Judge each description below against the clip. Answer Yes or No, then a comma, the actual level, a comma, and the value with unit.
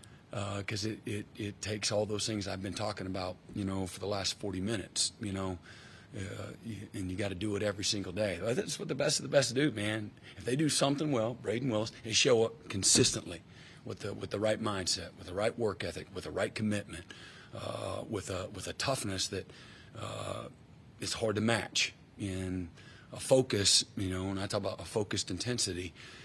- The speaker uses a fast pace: Yes, fast, 215 wpm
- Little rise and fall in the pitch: No, average, 3.1 semitones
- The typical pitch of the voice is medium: No, low, 105 Hz